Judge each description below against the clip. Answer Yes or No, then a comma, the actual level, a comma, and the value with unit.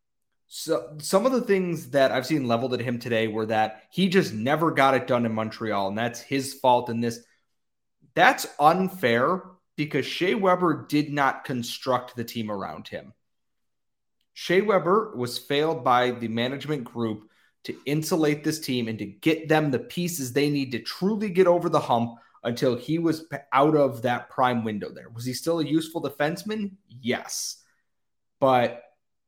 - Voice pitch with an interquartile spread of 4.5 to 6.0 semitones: Yes, average, 5.1 semitones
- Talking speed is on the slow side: No, average, 170 wpm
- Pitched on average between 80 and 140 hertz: Yes, low, 135 Hz